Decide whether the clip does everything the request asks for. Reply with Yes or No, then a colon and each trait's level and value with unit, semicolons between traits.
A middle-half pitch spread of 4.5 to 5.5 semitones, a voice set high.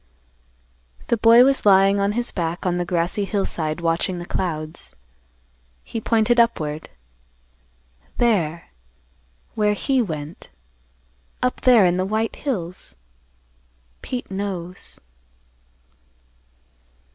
Yes: average, 4.9 semitones; high, 195 Hz